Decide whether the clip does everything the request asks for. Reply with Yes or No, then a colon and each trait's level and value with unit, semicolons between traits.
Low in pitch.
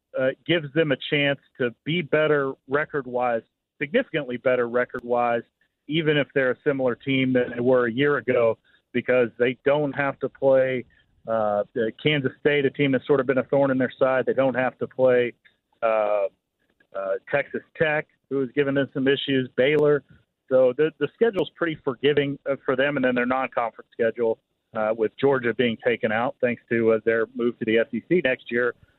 Yes: low, 130 Hz